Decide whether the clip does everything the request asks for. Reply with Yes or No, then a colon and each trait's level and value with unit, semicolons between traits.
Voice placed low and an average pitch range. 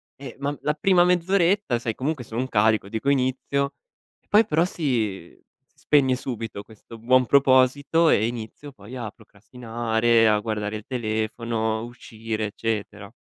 Yes: low, 120 Hz; average, 4.1 semitones